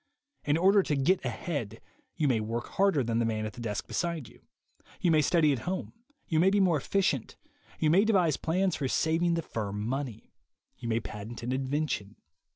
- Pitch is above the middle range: No, medium, 145 Hz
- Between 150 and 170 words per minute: No, average, 195 wpm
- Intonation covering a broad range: Yes, wide, 6.8 semitones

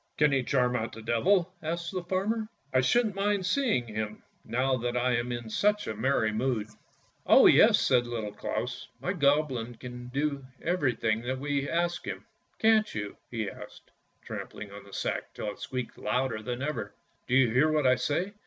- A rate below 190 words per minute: No, average, 200 wpm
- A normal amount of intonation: No, wide, 6.3 semitones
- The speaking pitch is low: Yes, low, 130 Hz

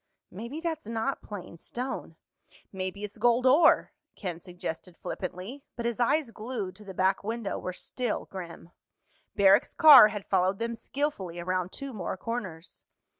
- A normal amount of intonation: Yes, average, 4.6 semitones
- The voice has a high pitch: Yes, high, 210 Hz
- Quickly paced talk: No, average, 145 wpm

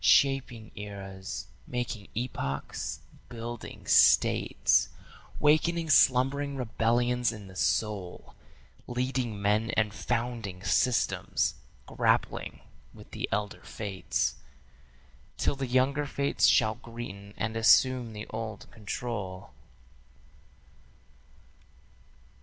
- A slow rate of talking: Yes, slow, 90 wpm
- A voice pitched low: Yes, low, 115 Hz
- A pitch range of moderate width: Yes, average, 3.6 semitones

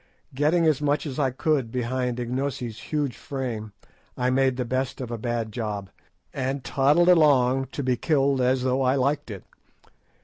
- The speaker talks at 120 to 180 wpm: Yes, average, 170 wpm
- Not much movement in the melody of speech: Yes, narrow, 2.3 semitones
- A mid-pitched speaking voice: No, low, 130 Hz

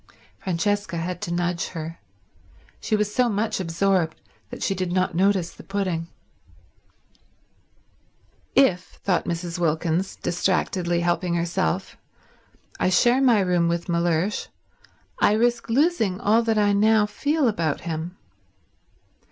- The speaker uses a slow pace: Yes, slow, 120 wpm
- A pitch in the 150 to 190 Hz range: Yes, medium, 185 Hz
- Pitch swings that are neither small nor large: Yes, average, 3.5 semitones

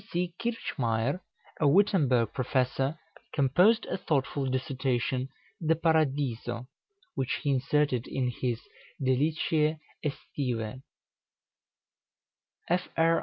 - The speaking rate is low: Yes, slow, 80 wpm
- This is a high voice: No, low, 135 Hz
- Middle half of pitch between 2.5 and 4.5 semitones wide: Yes, average, 3.8 semitones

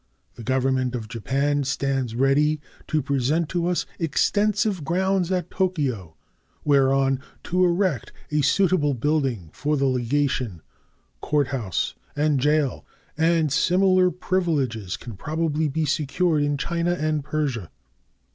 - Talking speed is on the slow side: Yes, slow, 125 wpm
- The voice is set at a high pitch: No, medium, 145 Hz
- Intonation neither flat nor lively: Yes, average, 4.1 semitones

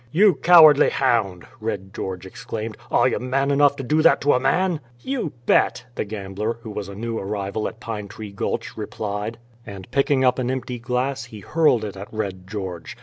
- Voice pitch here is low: Yes, low, 115 Hz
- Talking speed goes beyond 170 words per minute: Yes, average, 195 wpm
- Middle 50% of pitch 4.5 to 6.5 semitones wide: Yes, average, 5.2 semitones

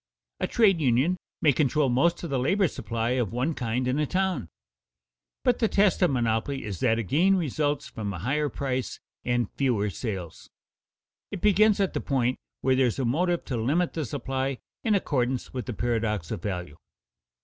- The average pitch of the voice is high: No, low, 130 Hz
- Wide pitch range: Yes, wide, 5.7 semitones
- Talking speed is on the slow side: No, average, 185 wpm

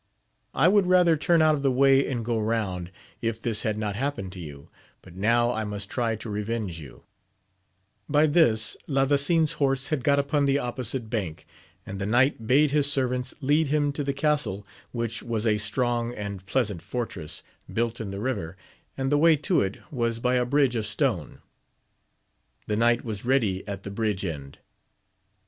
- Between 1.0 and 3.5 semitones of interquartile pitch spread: No, average, 5.0 semitones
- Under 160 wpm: No, average, 180 wpm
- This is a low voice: Yes, low, 120 Hz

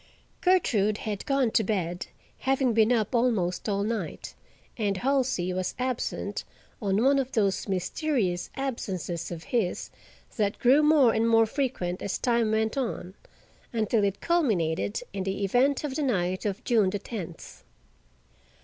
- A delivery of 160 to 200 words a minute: No, average, 150 wpm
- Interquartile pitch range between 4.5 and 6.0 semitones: Yes, average, 5.0 semitones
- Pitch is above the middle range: Yes, high, 220 Hz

